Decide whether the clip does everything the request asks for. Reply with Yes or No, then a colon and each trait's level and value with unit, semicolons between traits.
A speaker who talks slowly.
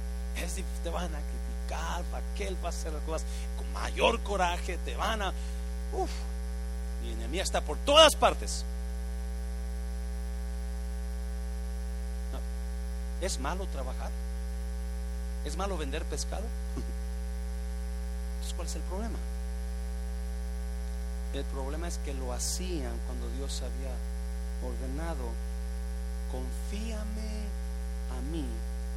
Yes: slow, 105 wpm